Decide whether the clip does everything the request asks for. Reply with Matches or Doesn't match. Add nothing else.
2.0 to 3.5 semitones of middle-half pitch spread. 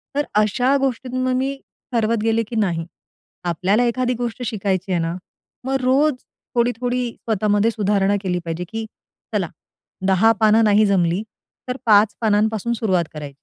Doesn't match